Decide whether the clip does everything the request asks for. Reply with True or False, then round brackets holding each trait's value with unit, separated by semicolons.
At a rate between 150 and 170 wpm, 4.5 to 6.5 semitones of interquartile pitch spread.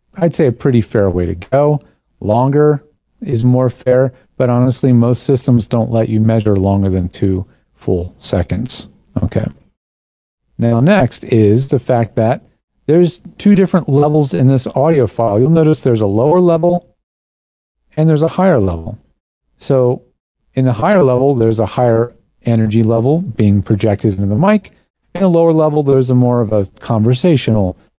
True (165 wpm; 5.5 semitones)